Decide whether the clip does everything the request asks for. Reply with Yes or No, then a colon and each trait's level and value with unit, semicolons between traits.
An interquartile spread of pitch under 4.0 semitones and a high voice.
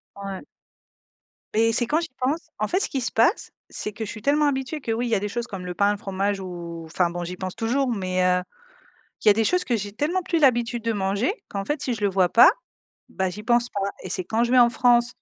No: average, 4.5 semitones; high, 225 Hz